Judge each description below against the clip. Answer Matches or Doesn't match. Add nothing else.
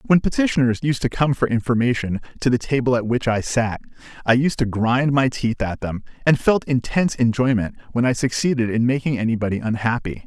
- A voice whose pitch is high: Doesn't match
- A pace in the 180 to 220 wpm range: Matches